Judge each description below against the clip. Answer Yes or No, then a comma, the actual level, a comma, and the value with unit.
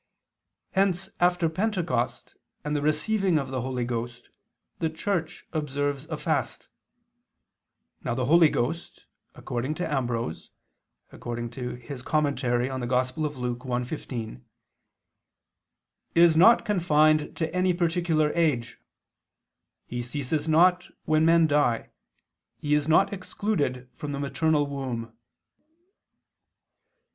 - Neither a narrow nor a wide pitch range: Yes, average, 4.8 semitones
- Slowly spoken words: Yes, slow, 100 wpm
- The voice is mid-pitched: Yes, medium, 150 Hz